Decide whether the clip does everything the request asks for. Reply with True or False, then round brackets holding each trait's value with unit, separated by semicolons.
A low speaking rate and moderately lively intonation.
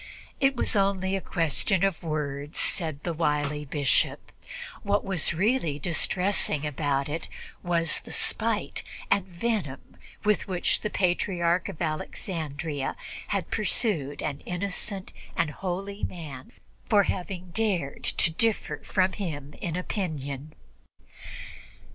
True (125 wpm; 4.7 semitones)